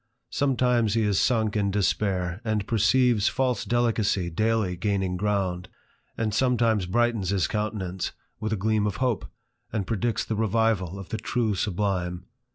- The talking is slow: No, average, 155 wpm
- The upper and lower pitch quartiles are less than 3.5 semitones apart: Yes, average, 3.0 semitones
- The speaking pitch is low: Yes, low, 105 Hz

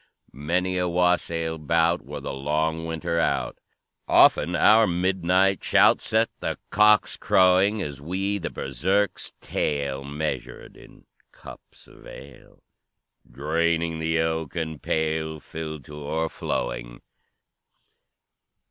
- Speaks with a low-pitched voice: Yes, very low, 80 Hz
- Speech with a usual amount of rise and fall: Yes, average, 3.1 semitones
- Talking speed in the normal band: No, slow, 110 wpm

